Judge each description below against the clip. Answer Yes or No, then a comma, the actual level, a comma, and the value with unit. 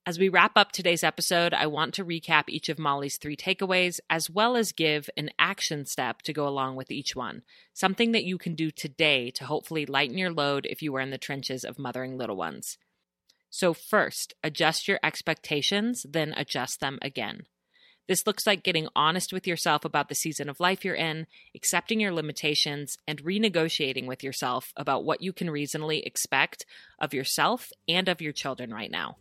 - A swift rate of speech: No, average, 190 wpm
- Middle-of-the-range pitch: Yes, medium, 155 Hz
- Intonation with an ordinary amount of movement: Yes, average, 4.0 semitones